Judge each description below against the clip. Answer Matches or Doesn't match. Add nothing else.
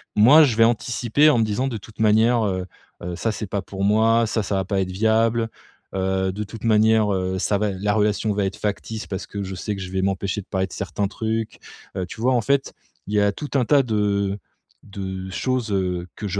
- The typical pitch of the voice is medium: Doesn't match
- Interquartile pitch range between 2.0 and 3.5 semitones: Matches